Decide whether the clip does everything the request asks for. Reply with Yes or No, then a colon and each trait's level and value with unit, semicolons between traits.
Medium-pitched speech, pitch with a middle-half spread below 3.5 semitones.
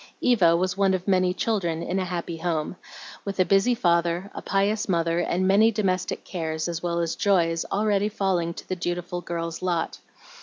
Yes: medium, 180 Hz; narrow, 2.5 semitones